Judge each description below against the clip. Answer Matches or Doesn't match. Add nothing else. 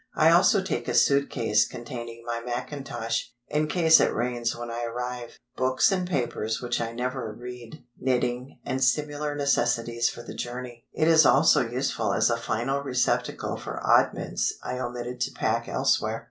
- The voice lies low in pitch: Matches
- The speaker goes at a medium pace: Matches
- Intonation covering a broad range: Doesn't match